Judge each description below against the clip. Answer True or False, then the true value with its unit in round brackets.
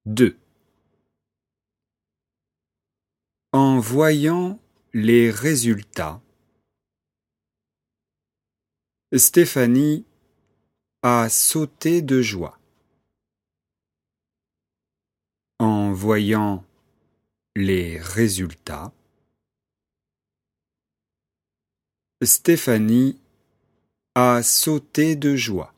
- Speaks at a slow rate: True (45 wpm)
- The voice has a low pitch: True (115 Hz)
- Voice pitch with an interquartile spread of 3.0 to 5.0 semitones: False (5.6 semitones)